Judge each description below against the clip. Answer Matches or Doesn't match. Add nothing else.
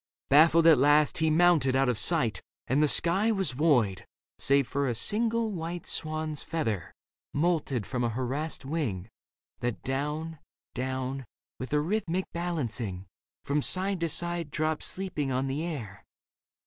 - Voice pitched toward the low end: Doesn't match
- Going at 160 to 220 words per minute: Doesn't match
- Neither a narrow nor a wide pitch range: Matches